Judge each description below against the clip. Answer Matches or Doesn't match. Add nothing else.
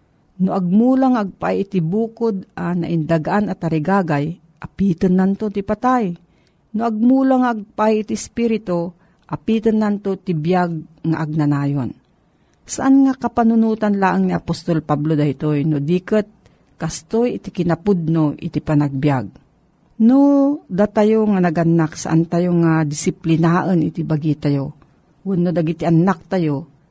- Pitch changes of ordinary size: Matches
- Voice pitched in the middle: Matches